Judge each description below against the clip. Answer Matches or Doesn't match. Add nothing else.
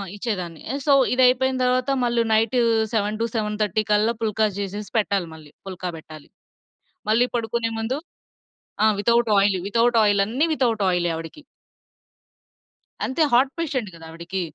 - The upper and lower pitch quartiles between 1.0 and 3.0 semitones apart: Doesn't match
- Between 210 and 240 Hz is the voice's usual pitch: Matches